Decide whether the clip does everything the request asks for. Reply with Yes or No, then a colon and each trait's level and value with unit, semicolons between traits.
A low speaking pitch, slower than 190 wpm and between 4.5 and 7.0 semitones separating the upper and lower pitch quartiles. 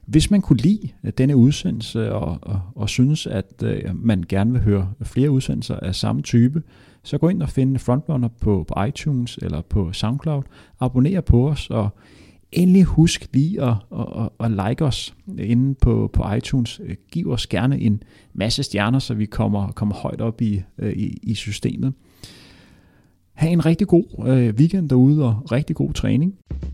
Yes: low, 120 Hz; average, 165 wpm; average, 5.3 semitones